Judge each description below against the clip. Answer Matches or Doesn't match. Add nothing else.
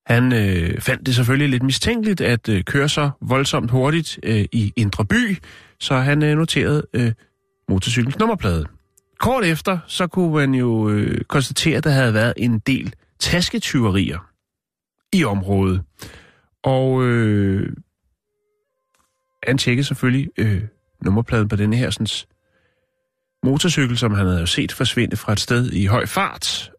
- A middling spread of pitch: Doesn't match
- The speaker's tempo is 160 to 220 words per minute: Doesn't match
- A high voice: Doesn't match